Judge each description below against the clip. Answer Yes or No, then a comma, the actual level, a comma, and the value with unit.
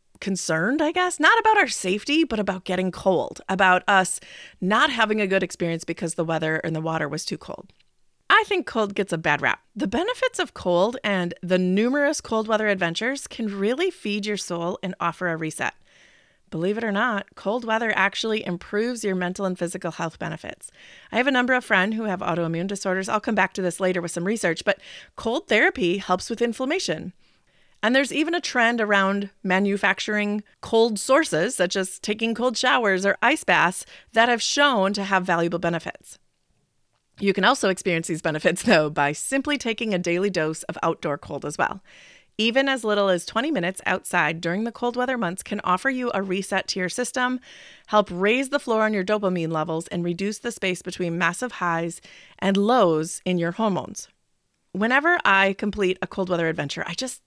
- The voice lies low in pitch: No, high, 195 Hz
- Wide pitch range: No, average, 4.5 semitones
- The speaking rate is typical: Yes, average, 190 wpm